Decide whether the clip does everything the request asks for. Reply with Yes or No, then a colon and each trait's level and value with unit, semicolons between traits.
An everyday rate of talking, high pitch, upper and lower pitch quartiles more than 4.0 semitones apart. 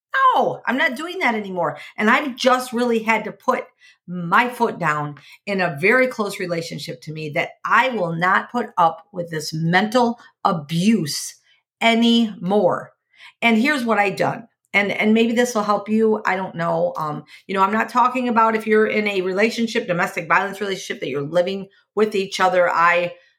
Yes: average, 180 wpm; high, 205 Hz; average, 4.7 semitones